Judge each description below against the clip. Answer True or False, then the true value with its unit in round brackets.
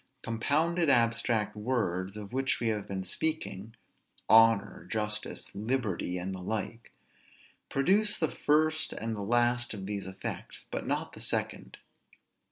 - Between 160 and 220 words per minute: False (135 wpm)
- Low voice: True (115 Hz)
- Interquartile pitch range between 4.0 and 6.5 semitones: True (4.5 semitones)